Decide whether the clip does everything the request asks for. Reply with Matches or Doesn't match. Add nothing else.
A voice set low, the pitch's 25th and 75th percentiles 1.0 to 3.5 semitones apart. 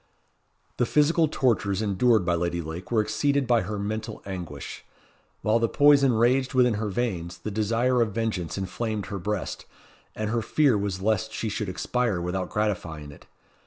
Doesn't match